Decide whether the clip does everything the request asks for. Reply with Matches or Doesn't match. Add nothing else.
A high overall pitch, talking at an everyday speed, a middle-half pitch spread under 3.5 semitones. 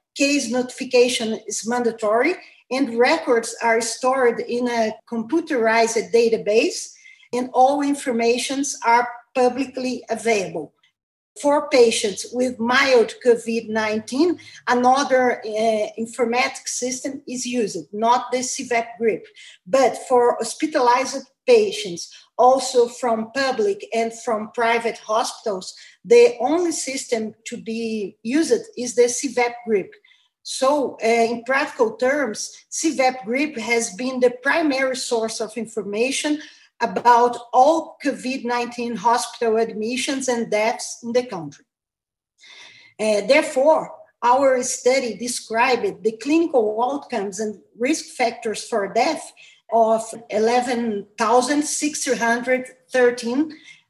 Doesn't match